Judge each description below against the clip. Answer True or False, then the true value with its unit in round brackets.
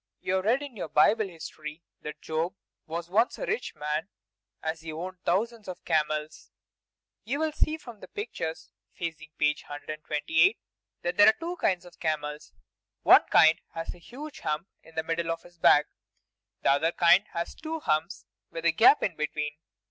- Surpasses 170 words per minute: True (180 wpm)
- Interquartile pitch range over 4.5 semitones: True (5.0 semitones)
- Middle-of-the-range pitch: True (170 Hz)